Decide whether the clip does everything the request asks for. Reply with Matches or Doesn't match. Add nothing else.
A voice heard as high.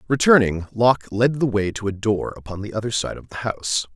Doesn't match